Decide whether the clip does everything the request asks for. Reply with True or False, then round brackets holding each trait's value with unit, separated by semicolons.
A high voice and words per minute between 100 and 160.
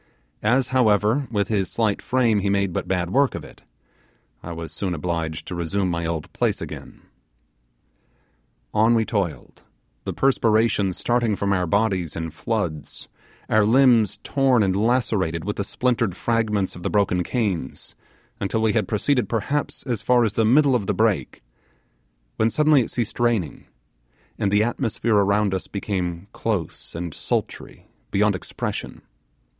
False (105 Hz; 155 wpm)